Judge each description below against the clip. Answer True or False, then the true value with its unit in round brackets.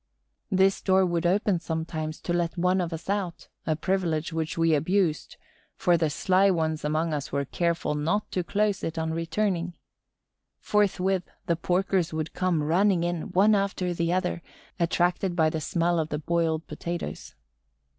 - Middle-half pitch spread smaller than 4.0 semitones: True (2.5 semitones)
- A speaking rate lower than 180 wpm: True (165 wpm)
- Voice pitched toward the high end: False (170 Hz)